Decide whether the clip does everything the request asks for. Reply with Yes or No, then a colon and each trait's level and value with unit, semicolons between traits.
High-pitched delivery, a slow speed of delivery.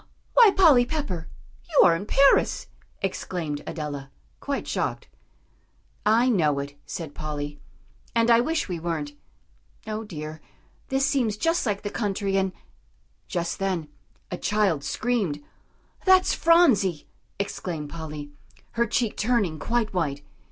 Yes: high, 195 Hz; slow, 130 wpm